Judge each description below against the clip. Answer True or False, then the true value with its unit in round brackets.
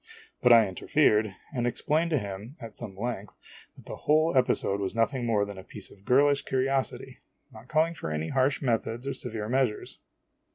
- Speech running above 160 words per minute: True (190 wpm)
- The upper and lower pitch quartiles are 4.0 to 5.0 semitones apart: True (4.5 semitones)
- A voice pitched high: False (120 Hz)